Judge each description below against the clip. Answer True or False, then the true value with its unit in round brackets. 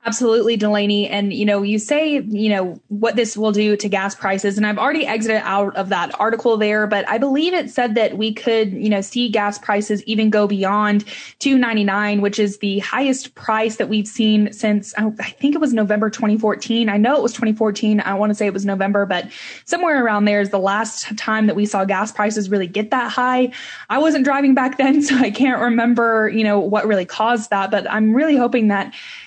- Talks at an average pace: False (215 wpm)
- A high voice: True (215 Hz)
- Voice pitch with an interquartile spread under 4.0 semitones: True (2.6 semitones)